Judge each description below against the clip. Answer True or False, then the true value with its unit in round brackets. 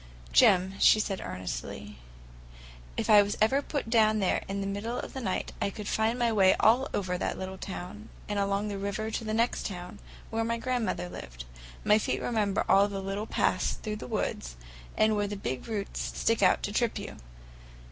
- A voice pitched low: False (205 Hz)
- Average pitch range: False (2.3 semitones)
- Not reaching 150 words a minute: False (195 wpm)